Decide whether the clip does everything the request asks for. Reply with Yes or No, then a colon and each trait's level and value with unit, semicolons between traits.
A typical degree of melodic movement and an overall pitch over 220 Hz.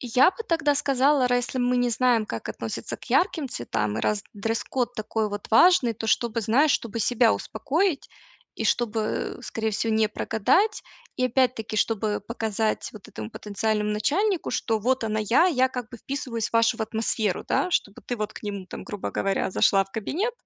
Yes: average, 3.3 semitones; high, 230 Hz